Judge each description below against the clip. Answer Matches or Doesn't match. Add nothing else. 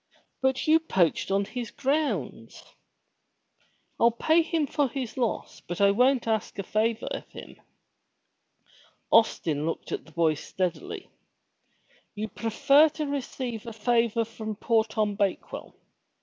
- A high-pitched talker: Matches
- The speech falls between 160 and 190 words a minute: Doesn't match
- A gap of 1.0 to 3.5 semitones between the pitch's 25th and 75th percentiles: Doesn't match